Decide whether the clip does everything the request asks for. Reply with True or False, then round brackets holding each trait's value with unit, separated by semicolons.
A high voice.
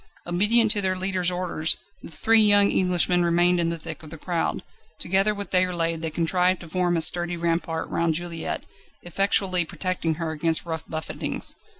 False (175 Hz)